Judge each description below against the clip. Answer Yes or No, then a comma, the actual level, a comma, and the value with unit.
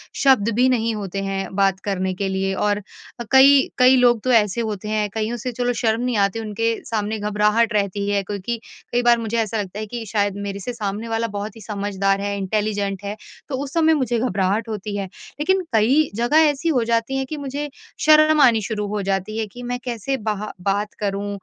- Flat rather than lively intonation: No, average, 3.2 semitones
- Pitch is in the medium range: No, high, 215 Hz